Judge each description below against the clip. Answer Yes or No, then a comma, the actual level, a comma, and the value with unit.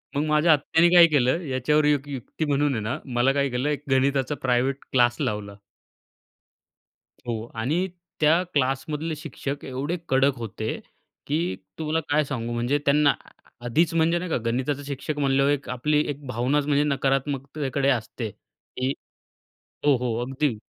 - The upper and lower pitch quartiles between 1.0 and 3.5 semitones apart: Yes, average, 2.7 semitones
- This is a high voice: No, medium, 140 Hz